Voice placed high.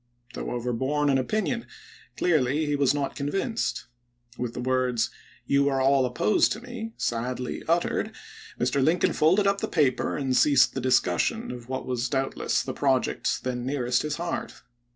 No: low, 135 Hz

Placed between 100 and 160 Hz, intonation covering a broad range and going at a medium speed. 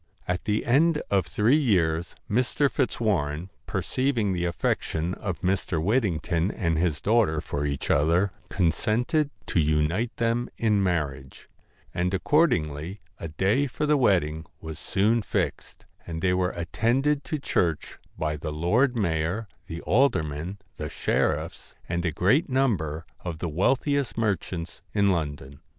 No: very low, 90 Hz; wide, 6.4 semitones; average, 145 wpm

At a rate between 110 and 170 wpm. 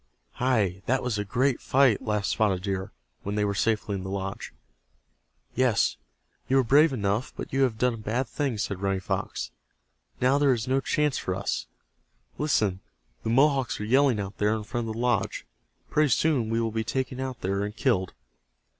No: average, 190 wpm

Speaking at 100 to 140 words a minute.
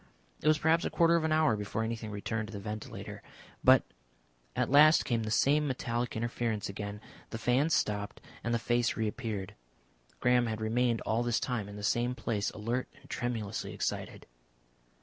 No: average, 175 wpm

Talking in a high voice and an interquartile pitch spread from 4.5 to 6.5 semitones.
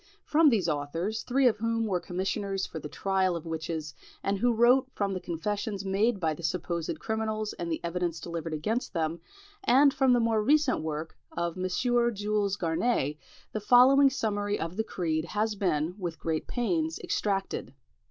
Yes: high, 195 Hz; average, 5.1 semitones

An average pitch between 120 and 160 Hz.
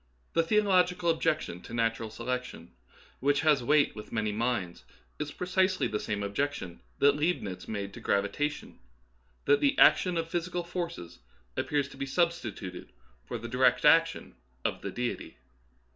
Yes: medium, 140 Hz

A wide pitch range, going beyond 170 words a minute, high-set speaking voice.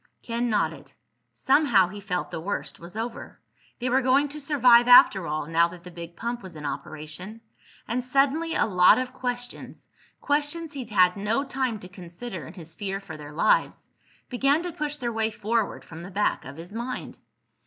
Yes: wide, 6.3 semitones; average, 180 wpm; high, 220 Hz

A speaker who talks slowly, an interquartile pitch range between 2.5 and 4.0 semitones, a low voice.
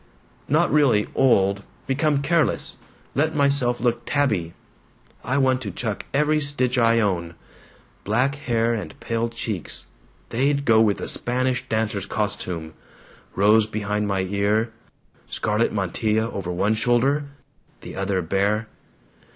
No: slow, 125 wpm; average, 4.4 semitones; low, 115 Hz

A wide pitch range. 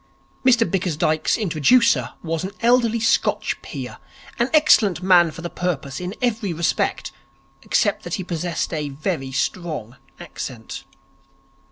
Yes: wide, 5.9 semitones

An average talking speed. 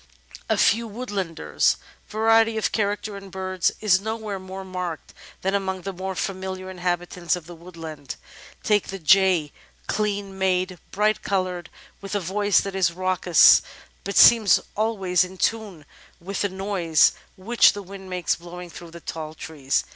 Yes: average, 155 wpm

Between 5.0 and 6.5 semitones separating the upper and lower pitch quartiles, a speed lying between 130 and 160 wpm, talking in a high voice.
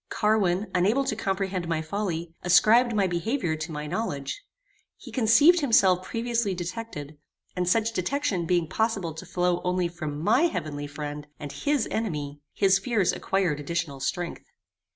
No: wide, 5.6 semitones; average, 150 wpm; medium, 180 Hz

